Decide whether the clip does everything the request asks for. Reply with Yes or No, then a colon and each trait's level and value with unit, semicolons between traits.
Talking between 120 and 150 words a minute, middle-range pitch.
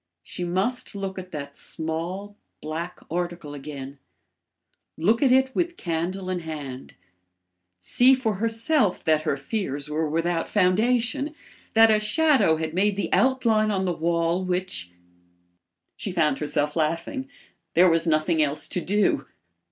Yes: average, 140 wpm; medium, 180 Hz